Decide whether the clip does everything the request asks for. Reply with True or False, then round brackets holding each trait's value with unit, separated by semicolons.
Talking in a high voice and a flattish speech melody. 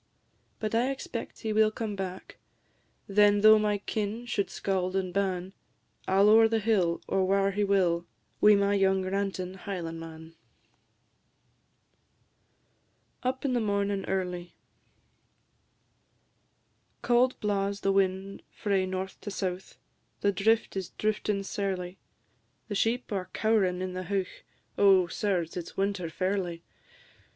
True (195 Hz; 2.1 semitones)